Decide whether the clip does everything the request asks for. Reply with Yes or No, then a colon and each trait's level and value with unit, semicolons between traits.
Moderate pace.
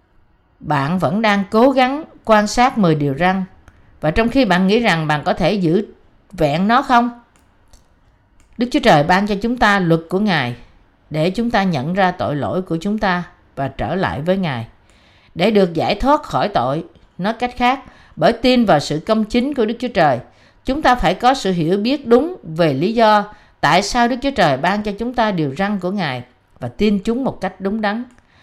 Yes: average, 205 wpm